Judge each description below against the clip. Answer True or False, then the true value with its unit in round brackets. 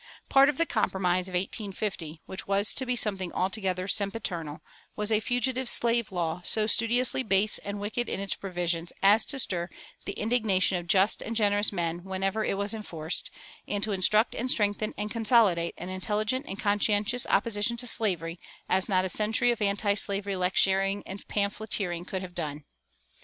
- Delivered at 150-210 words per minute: True (170 wpm)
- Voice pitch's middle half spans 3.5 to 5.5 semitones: False (2.9 semitones)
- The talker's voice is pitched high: True (200 Hz)